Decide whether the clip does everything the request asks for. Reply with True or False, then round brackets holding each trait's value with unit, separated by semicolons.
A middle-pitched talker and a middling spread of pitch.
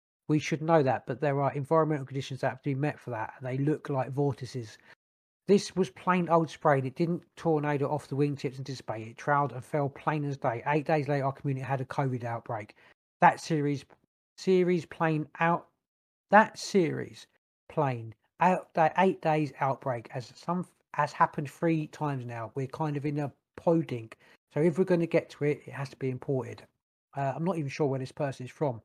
True (145 Hz; 3.4 semitones)